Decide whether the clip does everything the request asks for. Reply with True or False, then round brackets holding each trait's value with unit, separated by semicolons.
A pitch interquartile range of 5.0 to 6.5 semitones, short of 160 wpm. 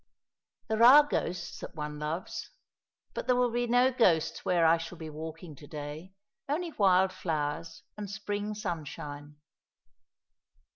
True (5.6 semitones; 140 wpm)